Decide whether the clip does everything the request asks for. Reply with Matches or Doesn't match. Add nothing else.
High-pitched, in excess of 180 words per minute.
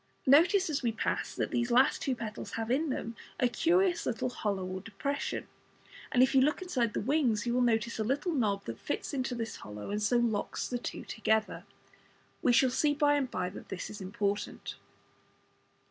Matches